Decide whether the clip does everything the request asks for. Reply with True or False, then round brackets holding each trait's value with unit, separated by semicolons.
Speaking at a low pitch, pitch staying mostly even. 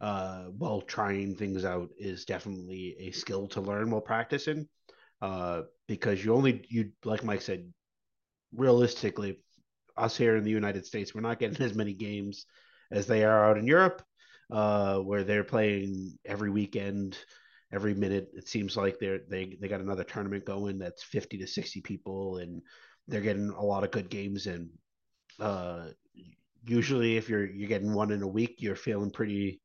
True (100 Hz; 2.0 semitones)